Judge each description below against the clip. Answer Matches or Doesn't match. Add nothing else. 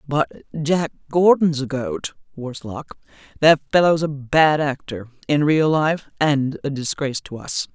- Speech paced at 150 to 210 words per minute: Doesn't match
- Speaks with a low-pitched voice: Doesn't match